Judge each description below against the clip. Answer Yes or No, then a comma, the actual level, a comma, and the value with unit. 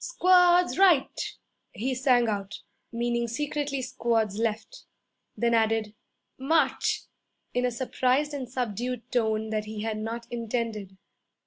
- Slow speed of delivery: Yes, slow, 120 wpm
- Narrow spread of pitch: No, average, 3.3 semitones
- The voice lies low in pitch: No, high, 235 Hz